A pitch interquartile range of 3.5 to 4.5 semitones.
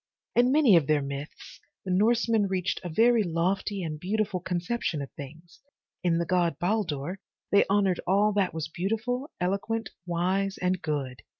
Yes: average, 3.9 semitones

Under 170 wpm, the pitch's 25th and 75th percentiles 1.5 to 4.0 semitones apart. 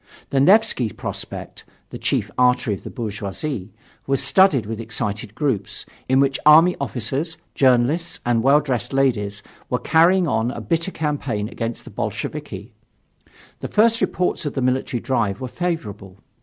No: average, 150 wpm; average, 5.2 semitones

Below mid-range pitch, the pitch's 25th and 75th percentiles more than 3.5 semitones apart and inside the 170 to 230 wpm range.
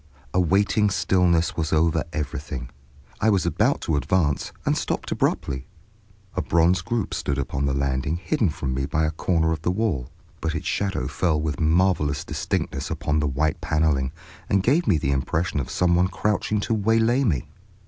Yes: very low, 80 Hz; average, 4.7 semitones; average, 180 wpm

